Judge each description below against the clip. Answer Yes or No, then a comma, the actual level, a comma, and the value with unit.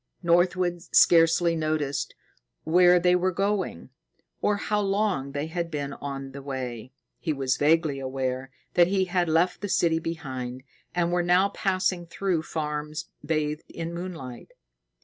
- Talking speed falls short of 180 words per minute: Yes, average, 145 wpm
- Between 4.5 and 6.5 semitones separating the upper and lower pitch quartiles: No, average, 3.9 semitones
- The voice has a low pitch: No, medium, 165 Hz